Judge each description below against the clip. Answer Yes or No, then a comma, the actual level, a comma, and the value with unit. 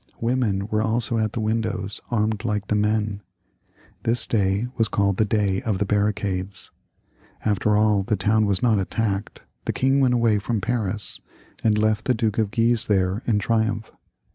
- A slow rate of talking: No, average, 170 wpm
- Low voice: Yes, low, 105 Hz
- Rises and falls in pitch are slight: Yes, narrow, 1.9 semitones